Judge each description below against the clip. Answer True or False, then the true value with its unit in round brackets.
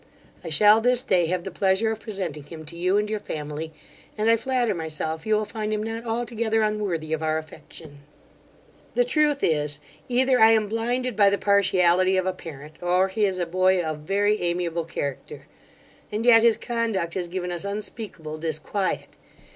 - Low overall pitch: False (190 Hz)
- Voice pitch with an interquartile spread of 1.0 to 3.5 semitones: False (4.9 semitones)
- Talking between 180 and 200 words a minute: True (185 wpm)